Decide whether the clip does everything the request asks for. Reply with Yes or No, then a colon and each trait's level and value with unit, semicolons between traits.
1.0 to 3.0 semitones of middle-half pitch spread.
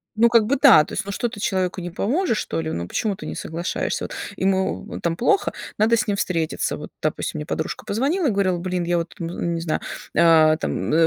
No: average, 4.8 semitones